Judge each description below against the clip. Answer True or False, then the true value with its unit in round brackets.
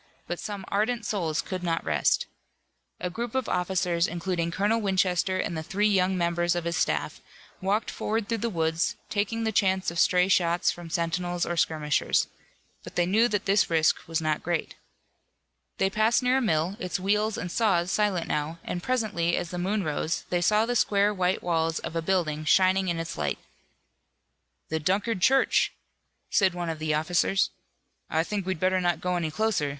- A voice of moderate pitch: True (180 Hz)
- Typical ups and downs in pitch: True (3.3 semitones)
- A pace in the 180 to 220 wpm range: True (185 wpm)